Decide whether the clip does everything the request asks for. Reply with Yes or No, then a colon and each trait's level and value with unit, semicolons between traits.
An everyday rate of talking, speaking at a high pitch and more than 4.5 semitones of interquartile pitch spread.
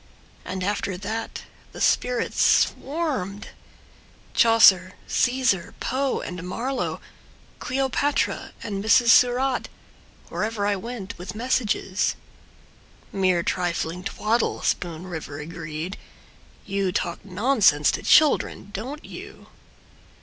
No: slow, 100 wpm; high, 205 Hz; average, 5.2 semitones